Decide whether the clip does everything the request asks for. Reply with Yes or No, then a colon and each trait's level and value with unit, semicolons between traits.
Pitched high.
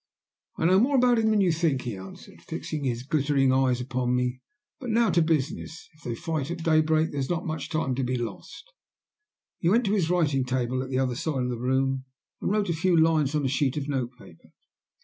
No: medium, 145 Hz